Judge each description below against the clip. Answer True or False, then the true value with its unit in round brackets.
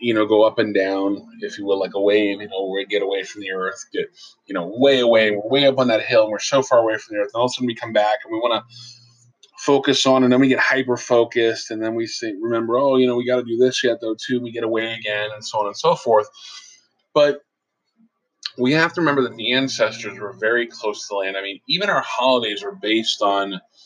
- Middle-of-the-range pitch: False (120 Hz)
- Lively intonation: False (3.9 semitones)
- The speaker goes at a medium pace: False (270 wpm)